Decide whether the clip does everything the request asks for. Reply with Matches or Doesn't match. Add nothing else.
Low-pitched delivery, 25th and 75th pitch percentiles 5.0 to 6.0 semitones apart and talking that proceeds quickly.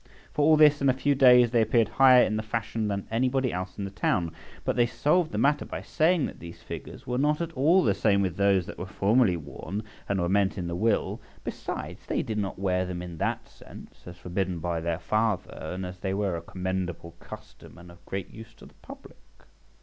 Matches